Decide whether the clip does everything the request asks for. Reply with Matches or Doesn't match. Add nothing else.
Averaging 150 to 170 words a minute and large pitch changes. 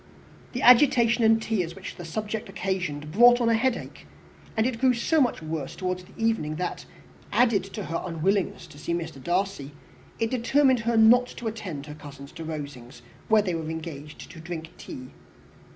Doesn't match